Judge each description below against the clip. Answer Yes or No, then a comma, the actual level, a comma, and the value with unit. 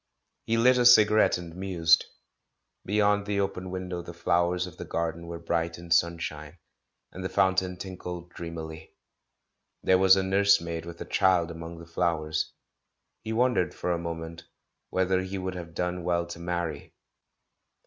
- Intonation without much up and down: Yes, narrow, 2.0 semitones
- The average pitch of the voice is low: Yes, very low, 90 Hz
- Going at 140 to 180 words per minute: Yes, average, 165 wpm